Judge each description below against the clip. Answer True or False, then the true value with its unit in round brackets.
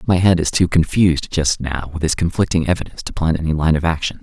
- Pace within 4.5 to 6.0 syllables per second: False (6.5 syllables/s)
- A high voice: False (85 Hz)